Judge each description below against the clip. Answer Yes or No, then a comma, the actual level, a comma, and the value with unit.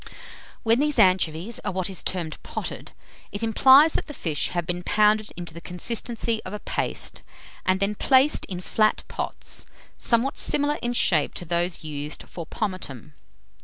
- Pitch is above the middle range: Yes, high, 195 Hz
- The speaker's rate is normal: Yes, average, 165 wpm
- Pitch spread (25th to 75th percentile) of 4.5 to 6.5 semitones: Yes, average, 5.1 semitones